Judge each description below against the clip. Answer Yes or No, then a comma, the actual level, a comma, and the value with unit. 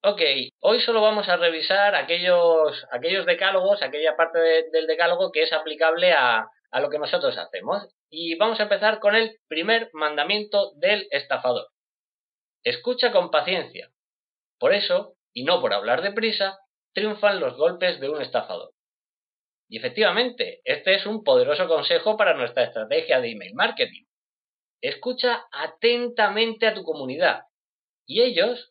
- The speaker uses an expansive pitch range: Yes, wide, 6.6 semitones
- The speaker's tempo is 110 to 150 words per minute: Yes, average, 145 wpm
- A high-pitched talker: Yes, high, 210 Hz